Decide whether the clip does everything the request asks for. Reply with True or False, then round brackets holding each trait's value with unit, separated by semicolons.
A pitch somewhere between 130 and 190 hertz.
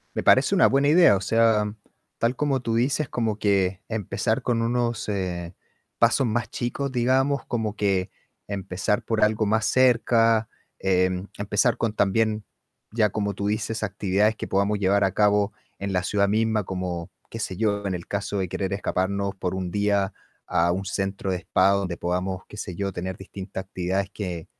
False (100 Hz)